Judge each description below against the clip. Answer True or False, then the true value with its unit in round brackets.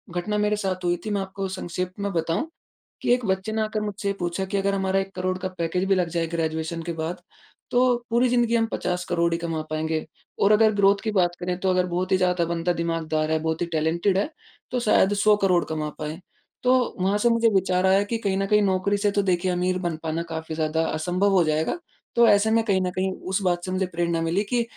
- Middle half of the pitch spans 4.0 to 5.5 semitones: False (3.1 semitones)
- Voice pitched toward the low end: False (185 Hz)